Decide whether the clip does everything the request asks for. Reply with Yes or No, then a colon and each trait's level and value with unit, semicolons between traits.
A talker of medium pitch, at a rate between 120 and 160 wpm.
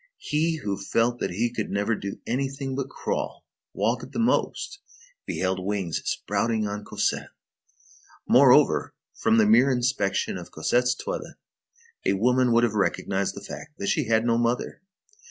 No: low, 115 Hz; average, 155 wpm